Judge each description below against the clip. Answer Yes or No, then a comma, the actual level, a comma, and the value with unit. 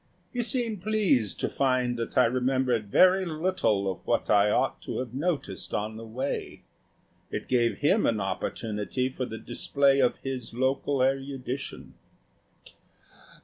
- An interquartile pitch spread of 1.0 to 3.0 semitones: No, average, 3.8 semitones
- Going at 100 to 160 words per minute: Yes, average, 145 wpm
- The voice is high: No, low, 130 Hz